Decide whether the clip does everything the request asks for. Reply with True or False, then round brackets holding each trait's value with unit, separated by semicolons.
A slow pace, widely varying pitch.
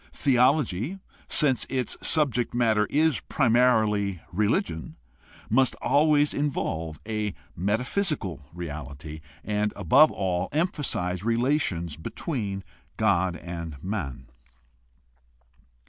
True (90 wpm; 7.2 semitones)